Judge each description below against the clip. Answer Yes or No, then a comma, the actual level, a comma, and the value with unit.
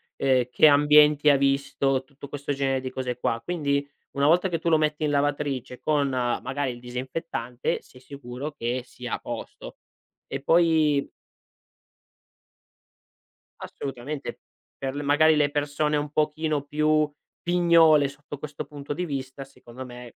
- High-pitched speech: No, medium, 145 Hz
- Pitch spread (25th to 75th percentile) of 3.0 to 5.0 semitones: No, narrow, 2.4 semitones